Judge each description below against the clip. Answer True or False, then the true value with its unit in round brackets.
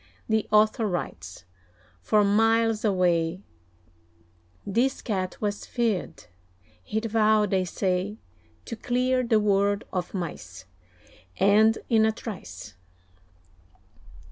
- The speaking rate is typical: False (100 wpm)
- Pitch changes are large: False (3.2 semitones)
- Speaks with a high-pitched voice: True (210 Hz)